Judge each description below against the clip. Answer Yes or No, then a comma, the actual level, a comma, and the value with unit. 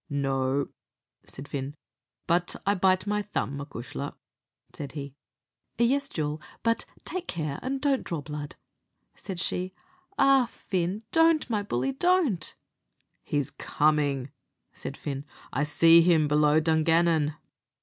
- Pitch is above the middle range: No, medium, 165 Hz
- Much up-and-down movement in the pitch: Yes, wide, 6.2 semitones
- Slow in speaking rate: Yes, slow, 125 wpm